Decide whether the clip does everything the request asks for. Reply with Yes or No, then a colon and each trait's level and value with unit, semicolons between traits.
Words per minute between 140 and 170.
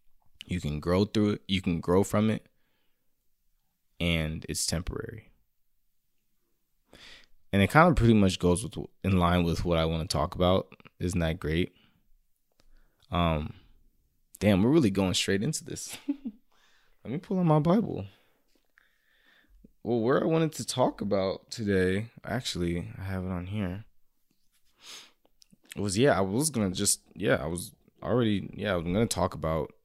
Yes: average, 155 wpm